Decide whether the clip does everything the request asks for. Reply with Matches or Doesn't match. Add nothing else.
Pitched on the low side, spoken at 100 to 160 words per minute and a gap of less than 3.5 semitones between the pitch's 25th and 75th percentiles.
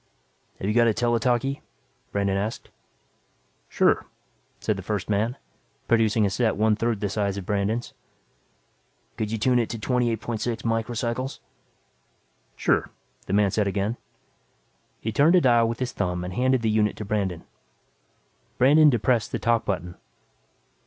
Matches